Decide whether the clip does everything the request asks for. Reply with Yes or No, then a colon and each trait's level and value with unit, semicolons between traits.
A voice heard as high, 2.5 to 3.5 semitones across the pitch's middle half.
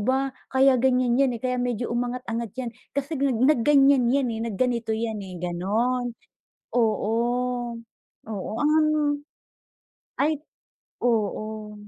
Yes: high, 245 Hz; average, 3.0 semitones